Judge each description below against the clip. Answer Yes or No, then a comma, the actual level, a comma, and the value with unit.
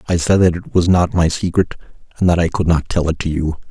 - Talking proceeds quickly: Yes, fast, 275 wpm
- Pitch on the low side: Yes, very low, 85 Hz